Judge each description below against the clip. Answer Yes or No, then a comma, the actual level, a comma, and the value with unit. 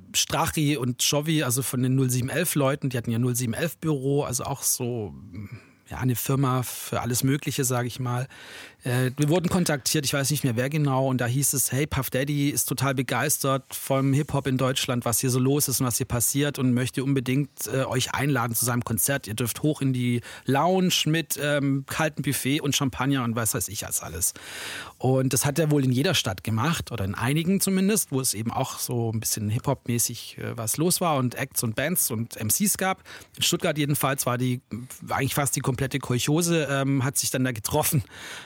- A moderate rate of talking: No, fast, 205 wpm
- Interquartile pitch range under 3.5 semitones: Yes, average, 2.9 semitones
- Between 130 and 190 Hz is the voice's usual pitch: Yes, low, 135 Hz